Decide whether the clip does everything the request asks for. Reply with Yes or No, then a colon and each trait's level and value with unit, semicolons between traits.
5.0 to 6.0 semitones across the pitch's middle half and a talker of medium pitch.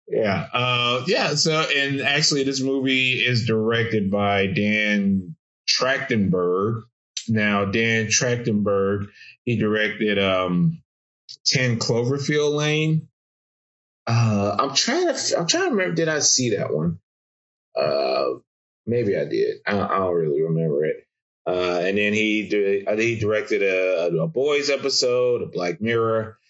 No: wide, 5.5 semitones; low, 115 Hz